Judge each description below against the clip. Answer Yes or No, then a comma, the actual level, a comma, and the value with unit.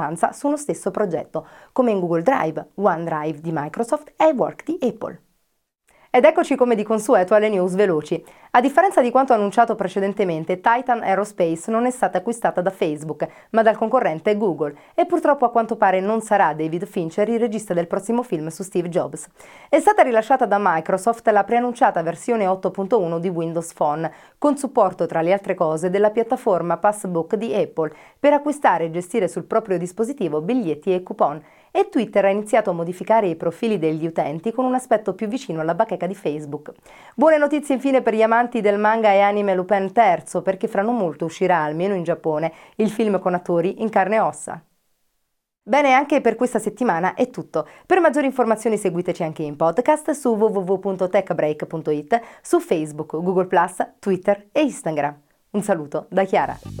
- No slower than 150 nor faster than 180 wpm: Yes, fast, 170 wpm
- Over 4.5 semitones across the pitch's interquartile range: Yes, wide, 5.5 semitones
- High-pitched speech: Yes, high, 200 Hz